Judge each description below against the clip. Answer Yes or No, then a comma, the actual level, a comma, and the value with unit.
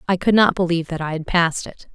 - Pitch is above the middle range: No, medium, 170 Hz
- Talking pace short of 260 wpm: No, fast, 280 wpm